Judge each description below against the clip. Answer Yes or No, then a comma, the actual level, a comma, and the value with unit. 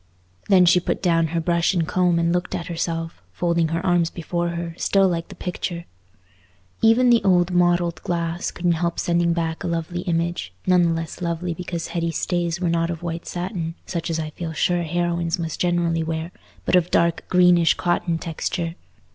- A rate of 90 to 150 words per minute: No, average, 185 wpm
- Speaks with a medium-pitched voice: Yes, medium, 170 Hz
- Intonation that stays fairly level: Yes, narrow, 1.1 semitones